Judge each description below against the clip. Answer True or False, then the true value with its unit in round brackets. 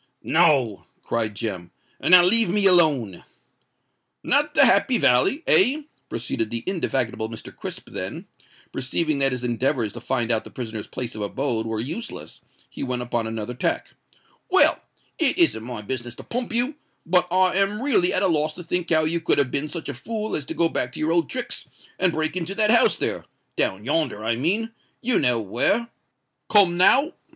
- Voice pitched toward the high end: False (155 Hz)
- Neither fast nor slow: True (180 wpm)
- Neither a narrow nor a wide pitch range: False (8.0 semitones)